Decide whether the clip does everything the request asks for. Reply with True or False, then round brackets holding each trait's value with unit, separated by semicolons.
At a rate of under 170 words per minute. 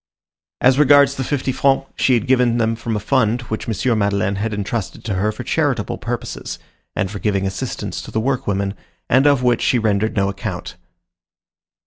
False (180 wpm)